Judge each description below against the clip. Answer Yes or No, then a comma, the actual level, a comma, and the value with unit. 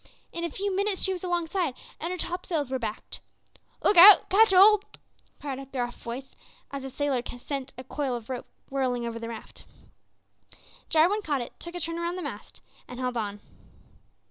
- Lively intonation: Yes, wide, 6.1 semitones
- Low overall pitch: No, very high, 290 Hz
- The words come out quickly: No, average, 185 wpm